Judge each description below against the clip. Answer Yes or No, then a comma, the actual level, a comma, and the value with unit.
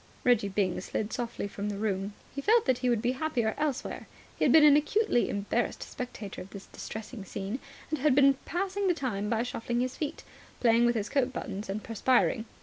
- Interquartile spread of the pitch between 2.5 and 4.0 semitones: No, average, 4.9 semitones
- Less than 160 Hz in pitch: No, high, 240 Hz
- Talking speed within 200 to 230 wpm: Yes, fast, 205 wpm